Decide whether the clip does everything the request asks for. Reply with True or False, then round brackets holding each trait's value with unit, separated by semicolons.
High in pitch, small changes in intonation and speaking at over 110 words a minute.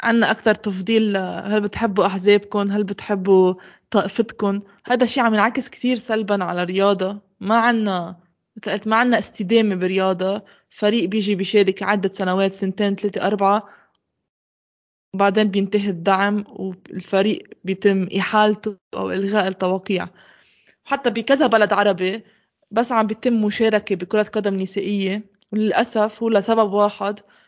True (205 Hz; 1.8 semitones; 120 wpm)